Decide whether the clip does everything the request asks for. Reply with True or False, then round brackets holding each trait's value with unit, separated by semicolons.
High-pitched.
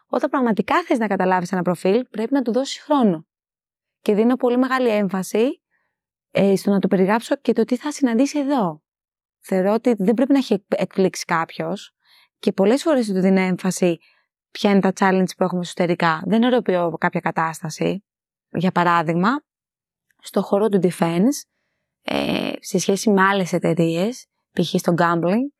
True (195 Hz)